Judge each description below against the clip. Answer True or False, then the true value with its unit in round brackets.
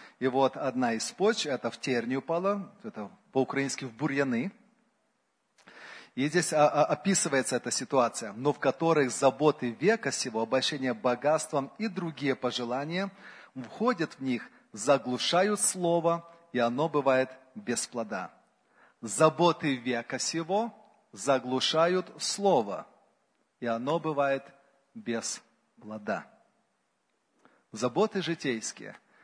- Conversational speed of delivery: False (105 wpm)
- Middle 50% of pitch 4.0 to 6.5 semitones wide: True (5.6 semitones)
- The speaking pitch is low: False (145 Hz)